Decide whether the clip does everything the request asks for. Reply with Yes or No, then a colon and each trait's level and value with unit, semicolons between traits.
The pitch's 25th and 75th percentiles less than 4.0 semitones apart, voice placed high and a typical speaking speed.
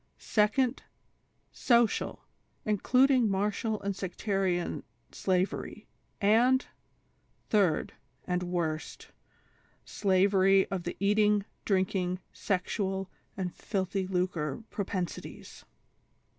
No: narrow, 2.4 semitones; high, 195 Hz; slow, 90 wpm